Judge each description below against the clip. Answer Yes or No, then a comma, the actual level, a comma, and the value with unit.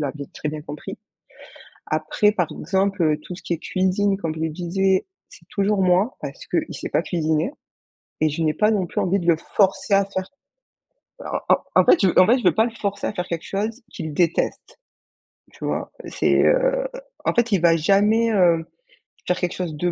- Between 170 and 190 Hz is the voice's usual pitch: Yes, medium, 185 Hz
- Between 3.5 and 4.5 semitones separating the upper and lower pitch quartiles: Yes, average, 3.8 semitones